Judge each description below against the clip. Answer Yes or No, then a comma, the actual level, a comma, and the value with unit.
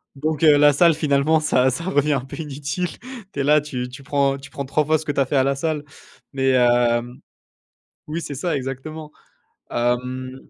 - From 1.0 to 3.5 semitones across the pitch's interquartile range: Yes, narrow, 2.6 semitones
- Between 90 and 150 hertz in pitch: Yes, medium, 140 Hz